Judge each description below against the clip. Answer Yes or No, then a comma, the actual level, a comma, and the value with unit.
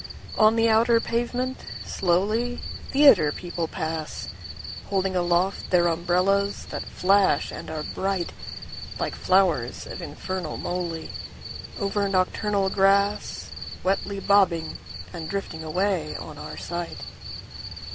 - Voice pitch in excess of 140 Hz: Yes, medium, 185 Hz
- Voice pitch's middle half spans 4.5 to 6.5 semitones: No, average, 3.3 semitones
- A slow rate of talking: Yes, slow, 95 wpm